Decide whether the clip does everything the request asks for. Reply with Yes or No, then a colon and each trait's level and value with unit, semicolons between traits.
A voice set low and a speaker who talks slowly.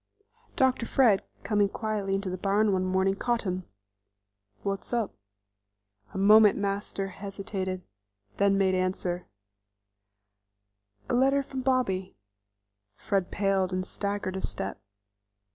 No: high, 195 Hz; slow, 115 wpm